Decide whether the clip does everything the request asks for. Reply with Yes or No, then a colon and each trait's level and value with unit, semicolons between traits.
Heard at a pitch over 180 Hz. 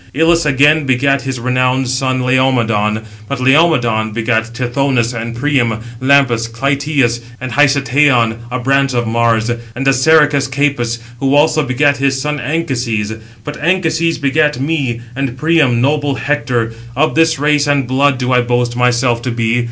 No: low, 130 Hz